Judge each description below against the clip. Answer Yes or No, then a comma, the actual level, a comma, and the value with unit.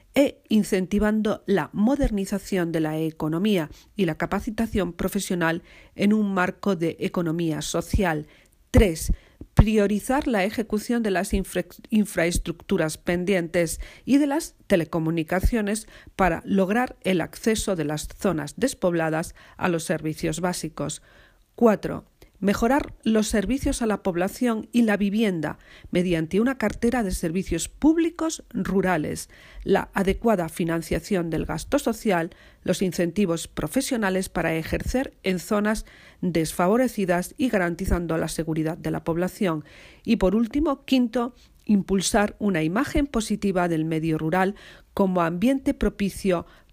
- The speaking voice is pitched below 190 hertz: No, high, 195 Hz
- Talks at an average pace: No, slow, 120 wpm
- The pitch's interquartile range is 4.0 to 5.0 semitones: Yes, average, 4.5 semitones